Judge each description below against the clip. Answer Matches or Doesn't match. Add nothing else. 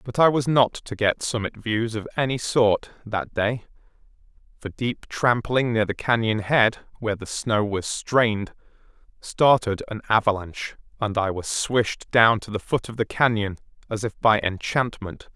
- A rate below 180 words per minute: Matches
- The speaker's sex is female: Doesn't match